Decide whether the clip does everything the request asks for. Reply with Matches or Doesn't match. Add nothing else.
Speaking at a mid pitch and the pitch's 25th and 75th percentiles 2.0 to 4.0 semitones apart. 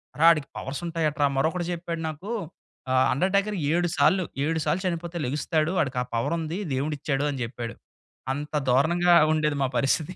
Matches